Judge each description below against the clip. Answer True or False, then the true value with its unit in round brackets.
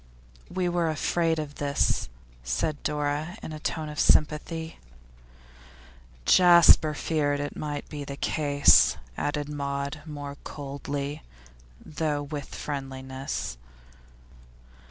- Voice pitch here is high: False (145 Hz)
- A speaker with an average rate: False (105 wpm)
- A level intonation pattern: True (1.6 semitones)